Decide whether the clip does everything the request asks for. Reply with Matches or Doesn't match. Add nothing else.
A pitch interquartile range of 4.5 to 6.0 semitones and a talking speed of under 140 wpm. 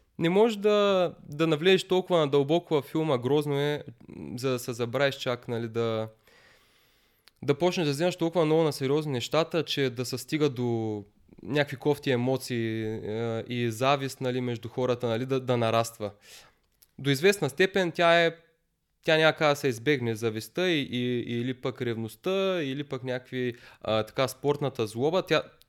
Doesn't match